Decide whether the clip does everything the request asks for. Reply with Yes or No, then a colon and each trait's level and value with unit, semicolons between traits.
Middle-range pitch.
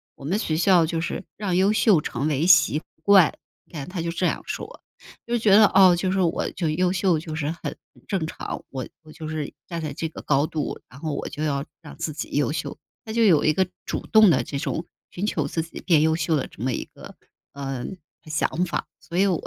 Yes: medium, 165 Hz